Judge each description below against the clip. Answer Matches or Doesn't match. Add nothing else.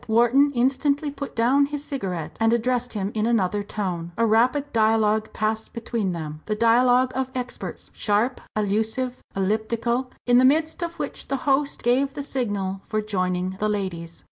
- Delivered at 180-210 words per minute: Doesn't match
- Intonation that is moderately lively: Matches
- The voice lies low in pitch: Doesn't match